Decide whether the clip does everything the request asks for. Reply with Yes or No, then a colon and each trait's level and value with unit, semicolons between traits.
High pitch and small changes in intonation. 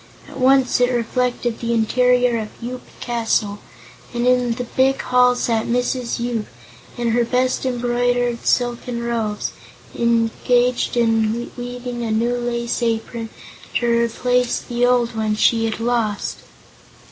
Yes: high, 240 Hz; narrow, 1.2 semitones